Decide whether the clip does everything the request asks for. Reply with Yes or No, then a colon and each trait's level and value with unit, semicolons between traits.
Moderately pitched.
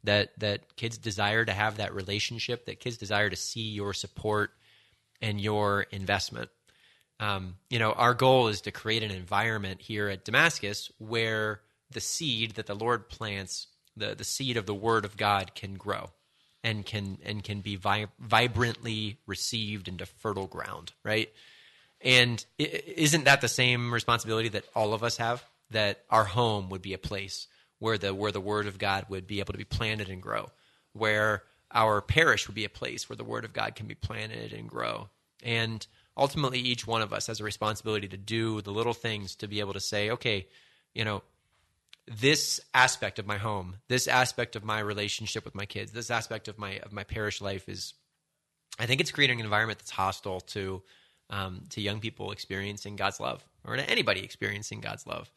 No: low, 105 Hz